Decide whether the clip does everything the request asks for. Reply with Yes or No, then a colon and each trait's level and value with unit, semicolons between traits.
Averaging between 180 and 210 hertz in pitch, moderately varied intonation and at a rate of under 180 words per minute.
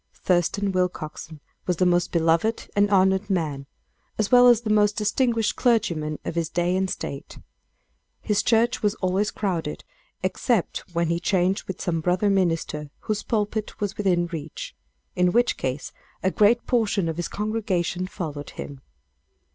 Yes: medium, 185 Hz; average, 3.8 semitones; average, 155 wpm